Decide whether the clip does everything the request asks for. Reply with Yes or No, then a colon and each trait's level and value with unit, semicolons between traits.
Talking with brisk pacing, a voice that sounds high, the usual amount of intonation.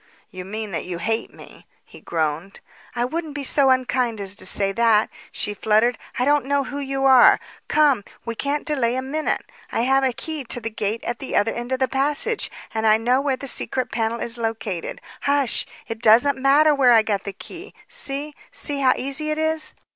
Yes: fast, 210 wpm; very high, 255 Hz; average, 4.2 semitones